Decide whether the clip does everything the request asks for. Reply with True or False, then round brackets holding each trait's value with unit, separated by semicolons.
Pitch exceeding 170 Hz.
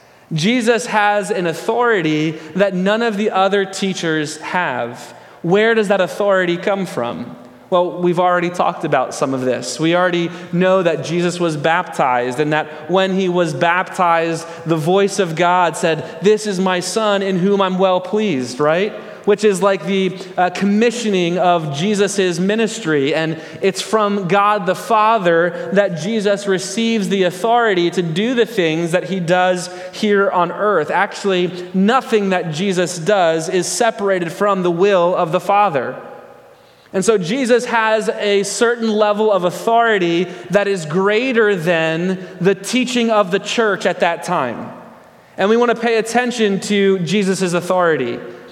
True (190 Hz)